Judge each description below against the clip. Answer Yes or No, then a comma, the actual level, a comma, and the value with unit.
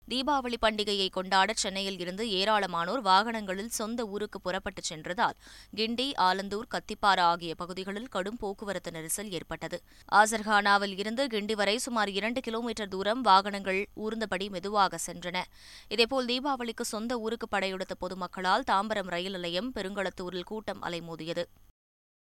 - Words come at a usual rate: Yes, average, 120 wpm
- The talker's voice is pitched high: Yes, high, 200 Hz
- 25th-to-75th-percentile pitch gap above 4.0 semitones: No, average, 3.2 semitones